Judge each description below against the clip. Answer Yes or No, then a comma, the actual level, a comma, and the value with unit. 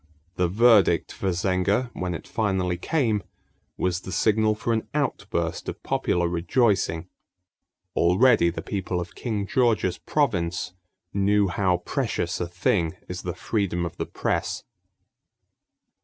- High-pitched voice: No, very low, 95 Hz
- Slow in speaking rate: Yes, slow, 130 wpm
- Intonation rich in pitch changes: No, average, 3.8 semitones